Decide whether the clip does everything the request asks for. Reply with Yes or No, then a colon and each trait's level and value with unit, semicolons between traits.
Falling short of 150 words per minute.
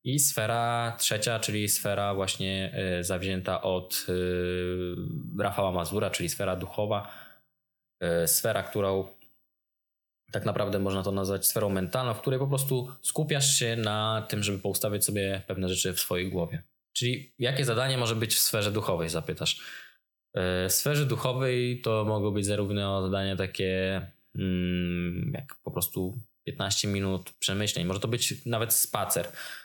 Yes: average, 135 wpm